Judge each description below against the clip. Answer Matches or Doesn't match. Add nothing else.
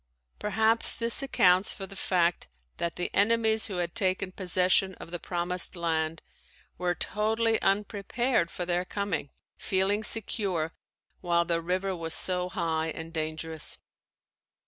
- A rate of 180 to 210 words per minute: Doesn't match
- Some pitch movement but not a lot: Matches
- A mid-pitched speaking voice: Matches